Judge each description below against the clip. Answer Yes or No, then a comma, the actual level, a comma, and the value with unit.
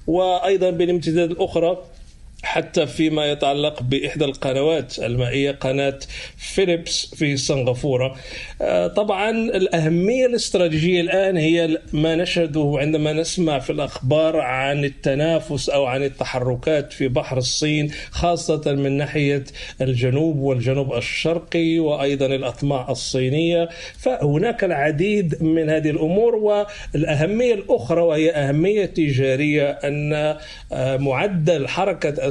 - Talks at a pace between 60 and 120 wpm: Yes, average, 100 wpm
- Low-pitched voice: No, medium, 155 Hz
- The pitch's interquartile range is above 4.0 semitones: No, average, 3.5 semitones